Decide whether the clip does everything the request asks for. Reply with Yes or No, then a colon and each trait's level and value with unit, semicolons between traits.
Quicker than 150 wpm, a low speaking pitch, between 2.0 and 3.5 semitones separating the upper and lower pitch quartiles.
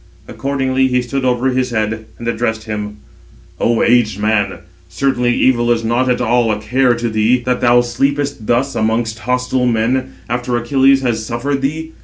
Yes: average, 170 wpm; low, 120 Hz; narrow, 2.6 semitones